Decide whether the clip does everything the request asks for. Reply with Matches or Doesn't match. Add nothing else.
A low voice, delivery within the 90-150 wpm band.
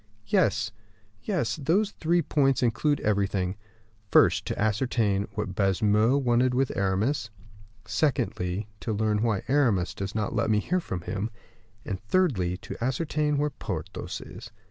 Matches